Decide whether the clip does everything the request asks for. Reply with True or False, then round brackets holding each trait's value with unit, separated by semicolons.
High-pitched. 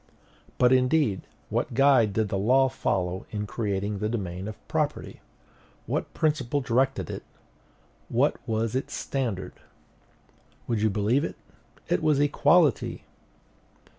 False (115 Hz)